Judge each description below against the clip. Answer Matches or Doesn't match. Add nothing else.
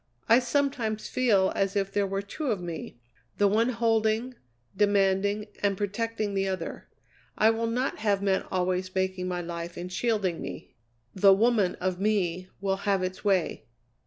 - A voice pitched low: Doesn't match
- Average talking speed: Matches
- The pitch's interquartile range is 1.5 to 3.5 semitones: Matches